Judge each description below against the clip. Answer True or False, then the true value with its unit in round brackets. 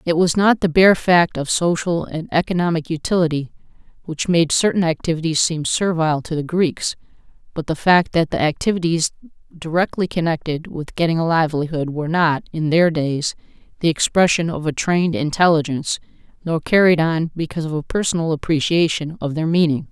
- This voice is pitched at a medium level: True (165 Hz)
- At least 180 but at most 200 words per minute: False (165 wpm)